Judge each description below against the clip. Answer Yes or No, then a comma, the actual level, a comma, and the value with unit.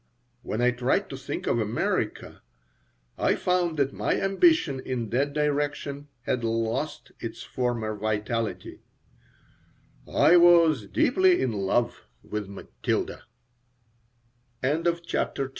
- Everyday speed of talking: No, slow, 120 wpm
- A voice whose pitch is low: Yes, low, 130 Hz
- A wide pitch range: Yes, wide, 6.0 semitones